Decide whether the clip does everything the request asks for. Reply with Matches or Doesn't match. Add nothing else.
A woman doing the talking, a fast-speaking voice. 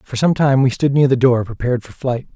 Doesn't match